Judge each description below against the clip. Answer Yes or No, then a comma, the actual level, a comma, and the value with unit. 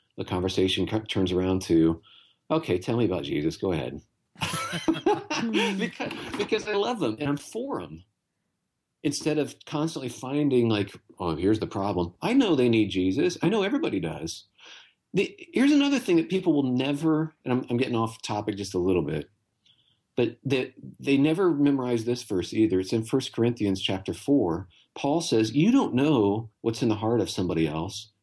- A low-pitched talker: Yes, low, 120 Hz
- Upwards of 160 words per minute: Yes, average, 175 wpm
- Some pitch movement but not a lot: No, wide, 7.3 semitones